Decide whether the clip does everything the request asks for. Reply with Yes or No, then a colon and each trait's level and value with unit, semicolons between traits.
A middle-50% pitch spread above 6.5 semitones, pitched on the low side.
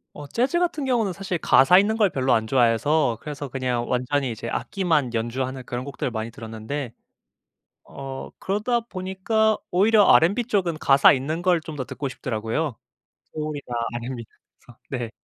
No: wide, 7.3 semitones; medium, 145 Hz